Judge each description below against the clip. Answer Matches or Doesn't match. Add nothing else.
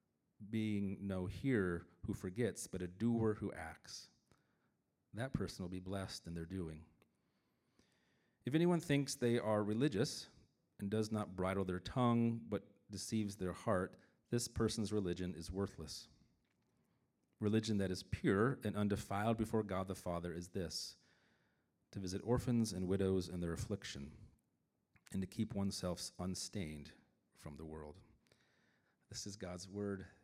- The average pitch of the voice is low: Matches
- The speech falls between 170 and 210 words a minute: Doesn't match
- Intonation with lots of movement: Doesn't match